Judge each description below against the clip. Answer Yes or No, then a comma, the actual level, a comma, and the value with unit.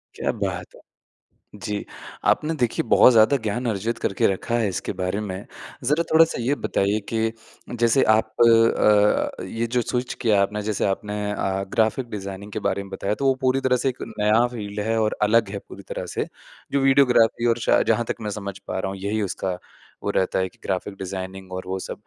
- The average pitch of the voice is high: No, low, 105 Hz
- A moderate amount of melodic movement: Yes, average, 3.4 semitones